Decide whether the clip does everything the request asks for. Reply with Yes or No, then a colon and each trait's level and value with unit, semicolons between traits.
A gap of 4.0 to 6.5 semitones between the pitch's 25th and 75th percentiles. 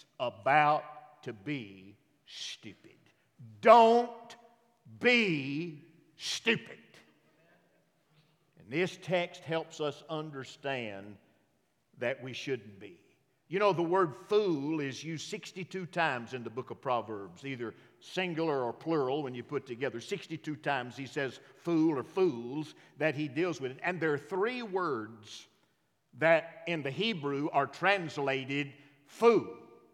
Yes: average, 4.6 semitones